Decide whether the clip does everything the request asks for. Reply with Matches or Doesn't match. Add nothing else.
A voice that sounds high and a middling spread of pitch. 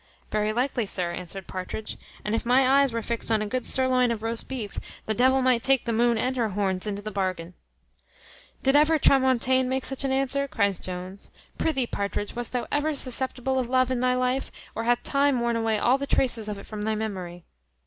Matches